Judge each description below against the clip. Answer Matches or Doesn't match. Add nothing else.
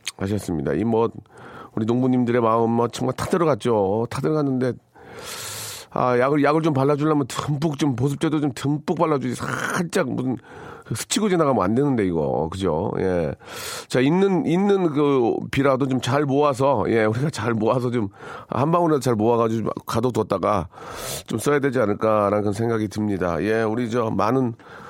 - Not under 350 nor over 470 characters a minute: Doesn't match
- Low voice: Matches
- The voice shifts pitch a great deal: Doesn't match